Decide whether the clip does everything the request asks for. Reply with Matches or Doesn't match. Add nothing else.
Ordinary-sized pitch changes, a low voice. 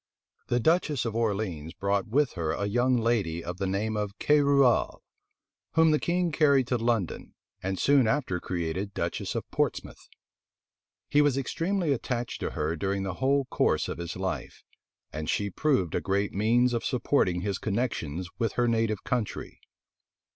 Doesn't match